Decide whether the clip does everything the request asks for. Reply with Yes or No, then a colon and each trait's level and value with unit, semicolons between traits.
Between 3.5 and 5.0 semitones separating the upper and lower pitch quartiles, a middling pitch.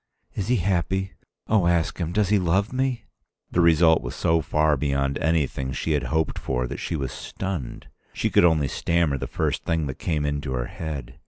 No: average, 4.0 semitones; very low, 80 Hz